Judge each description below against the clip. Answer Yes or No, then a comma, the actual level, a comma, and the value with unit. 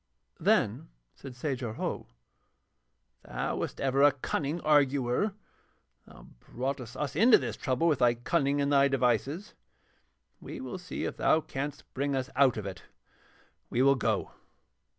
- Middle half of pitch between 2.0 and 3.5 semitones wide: Yes, average, 2.7 semitones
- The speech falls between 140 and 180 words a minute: Yes, average, 145 wpm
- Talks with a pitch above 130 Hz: Yes, medium, 140 Hz